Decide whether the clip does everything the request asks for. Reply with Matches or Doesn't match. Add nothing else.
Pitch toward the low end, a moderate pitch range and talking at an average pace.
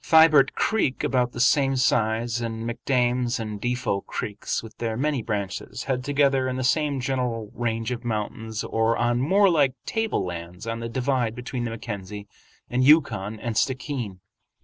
Matches